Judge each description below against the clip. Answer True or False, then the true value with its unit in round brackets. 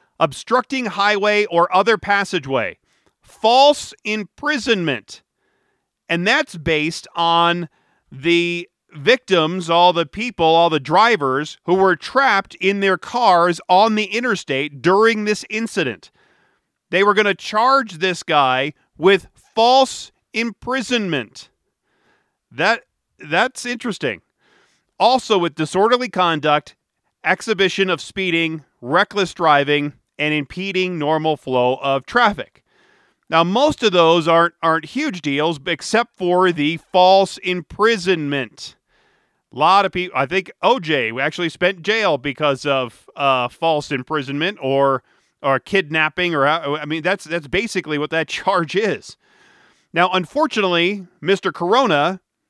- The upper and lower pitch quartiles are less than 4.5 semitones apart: False (5.1 semitones)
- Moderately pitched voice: True (180 Hz)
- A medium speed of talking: False (120 wpm)